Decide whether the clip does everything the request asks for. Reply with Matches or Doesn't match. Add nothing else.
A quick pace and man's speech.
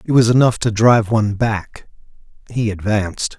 Doesn't match